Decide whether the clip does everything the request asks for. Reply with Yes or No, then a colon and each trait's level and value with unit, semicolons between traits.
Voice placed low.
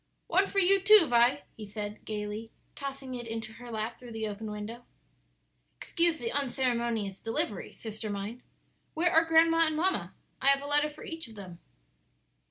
No: high, 240 Hz